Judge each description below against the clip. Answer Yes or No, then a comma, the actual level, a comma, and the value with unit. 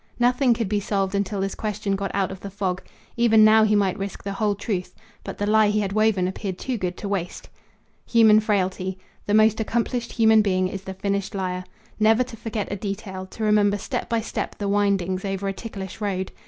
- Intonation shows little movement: Yes, narrow, 2.1 semitones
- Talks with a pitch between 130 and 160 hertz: No, high, 200 Hz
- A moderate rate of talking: No, fast, 210 wpm